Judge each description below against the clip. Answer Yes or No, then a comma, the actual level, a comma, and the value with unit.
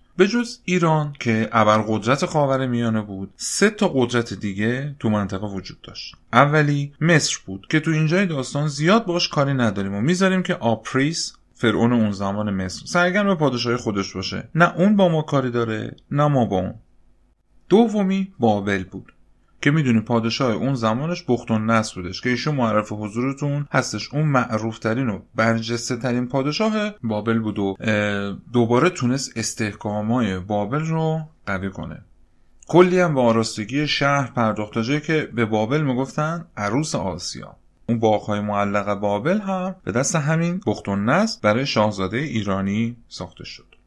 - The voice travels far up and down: Yes, wide, 6.2 semitones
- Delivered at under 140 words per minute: No, fast, 155 wpm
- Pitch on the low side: Yes, low, 120 Hz